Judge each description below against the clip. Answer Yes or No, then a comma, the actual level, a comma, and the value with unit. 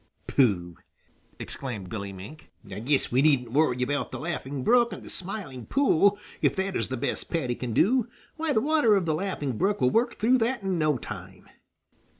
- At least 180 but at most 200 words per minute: Yes, average, 190 wpm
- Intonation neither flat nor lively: No, wide, 8.8 semitones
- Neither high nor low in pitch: Yes, medium, 155 Hz